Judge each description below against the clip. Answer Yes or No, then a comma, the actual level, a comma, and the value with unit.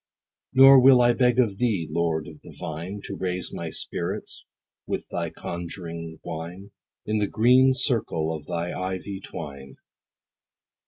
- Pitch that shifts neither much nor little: No, wide, 6.6 semitones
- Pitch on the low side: Yes, very low, 95 Hz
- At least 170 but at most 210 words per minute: No, average, 145 wpm